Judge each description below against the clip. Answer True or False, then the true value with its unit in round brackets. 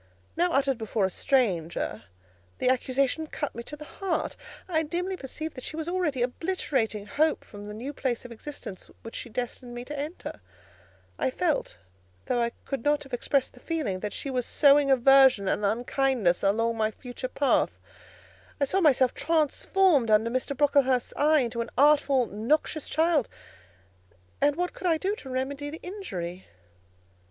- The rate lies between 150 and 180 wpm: True (165 wpm)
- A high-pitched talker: True (270 Hz)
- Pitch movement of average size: True (4.5 semitones)